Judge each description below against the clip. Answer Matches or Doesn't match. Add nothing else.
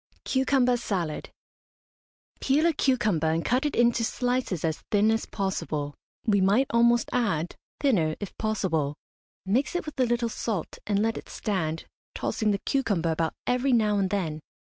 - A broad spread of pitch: Matches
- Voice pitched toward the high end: Matches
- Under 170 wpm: Matches